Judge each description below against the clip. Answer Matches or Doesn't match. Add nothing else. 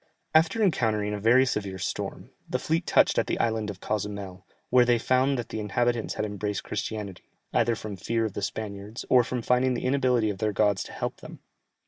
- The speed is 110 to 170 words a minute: Doesn't match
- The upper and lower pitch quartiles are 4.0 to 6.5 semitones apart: Doesn't match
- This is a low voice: Matches